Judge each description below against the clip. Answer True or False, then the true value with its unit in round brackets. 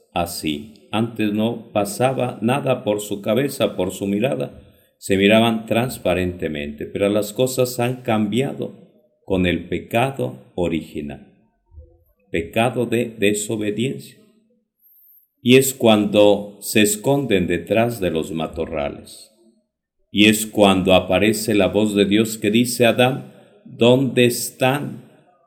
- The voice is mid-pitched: False (110 Hz)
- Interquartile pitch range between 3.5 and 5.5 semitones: True (4.0 semitones)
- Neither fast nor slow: False (115 wpm)